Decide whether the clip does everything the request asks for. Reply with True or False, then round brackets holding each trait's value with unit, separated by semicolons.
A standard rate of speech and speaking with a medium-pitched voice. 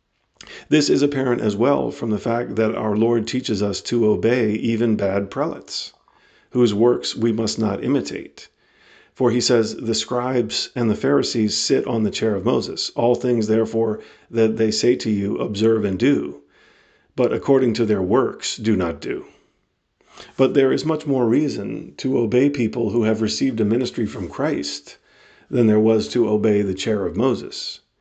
False (175 wpm; 115 Hz)